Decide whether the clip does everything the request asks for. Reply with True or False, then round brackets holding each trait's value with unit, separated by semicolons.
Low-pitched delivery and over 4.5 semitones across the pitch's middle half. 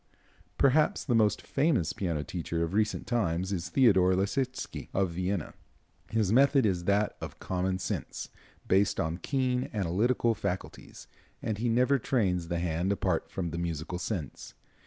True (95 Hz; 5.0 semitones)